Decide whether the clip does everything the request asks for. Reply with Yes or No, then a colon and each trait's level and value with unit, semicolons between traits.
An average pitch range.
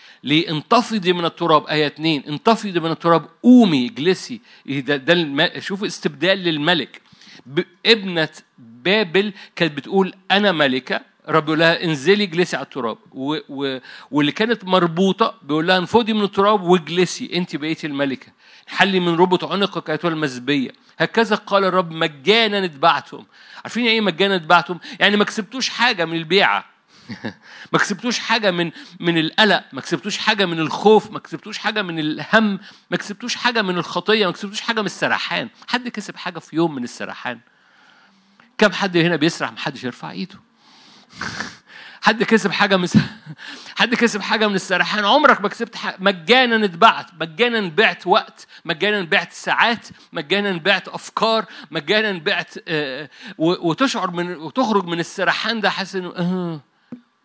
Yes: average, 4.3 semitones